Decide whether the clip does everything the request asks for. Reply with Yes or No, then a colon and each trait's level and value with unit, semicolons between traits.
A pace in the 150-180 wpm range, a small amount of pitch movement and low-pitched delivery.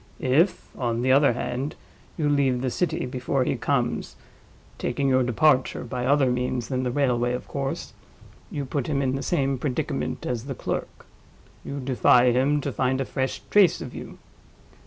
Yes: average, 170 wpm; narrow, 2.0 semitones; low, 130 Hz